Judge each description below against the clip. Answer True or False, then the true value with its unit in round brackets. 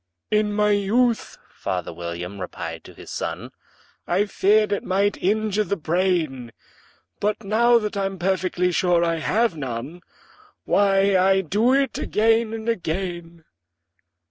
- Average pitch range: True (3.8 semitones)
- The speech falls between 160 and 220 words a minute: False (135 wpm)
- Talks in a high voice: True (195 Hz)